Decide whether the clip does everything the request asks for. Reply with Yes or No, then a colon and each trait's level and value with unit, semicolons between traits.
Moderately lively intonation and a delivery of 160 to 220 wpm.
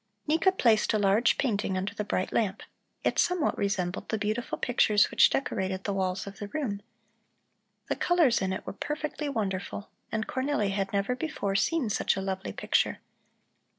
Yes: average, 4.9 semitones; average, 170 wpm